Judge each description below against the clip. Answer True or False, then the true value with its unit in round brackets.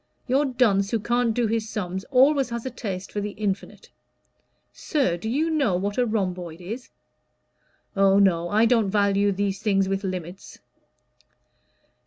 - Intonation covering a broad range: False (3.7 semitones)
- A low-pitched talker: False (205 Hz)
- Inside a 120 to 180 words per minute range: True (155 wpm)